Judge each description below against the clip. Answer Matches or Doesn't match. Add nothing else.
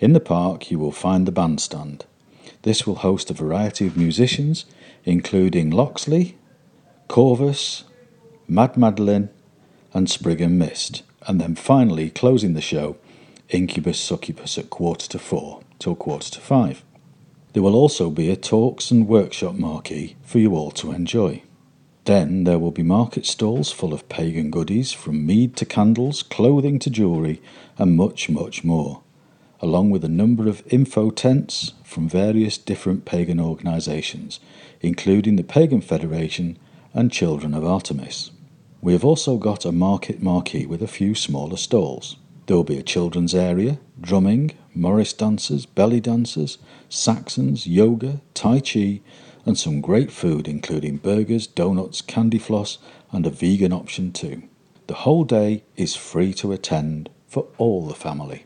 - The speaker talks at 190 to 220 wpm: Doesn't match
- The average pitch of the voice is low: Matches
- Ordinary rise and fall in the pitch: Doesn't match